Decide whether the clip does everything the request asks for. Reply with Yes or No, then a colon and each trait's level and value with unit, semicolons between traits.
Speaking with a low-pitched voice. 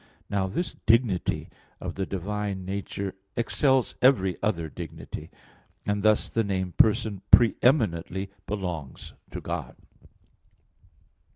Yes: low, 100 Hz